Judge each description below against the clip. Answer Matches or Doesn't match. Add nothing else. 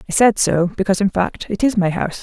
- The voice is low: Doesn't match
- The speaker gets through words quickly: Matches